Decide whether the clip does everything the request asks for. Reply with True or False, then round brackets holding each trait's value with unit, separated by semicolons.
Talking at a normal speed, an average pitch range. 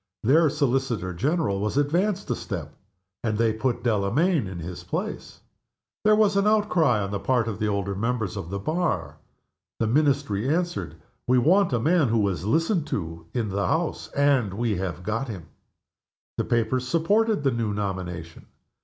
False (170 wpm; 7.8 semitones)